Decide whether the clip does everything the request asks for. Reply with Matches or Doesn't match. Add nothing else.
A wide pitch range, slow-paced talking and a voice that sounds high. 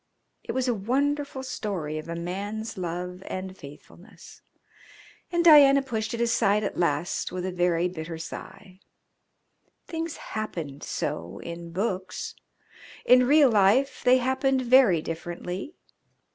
Matches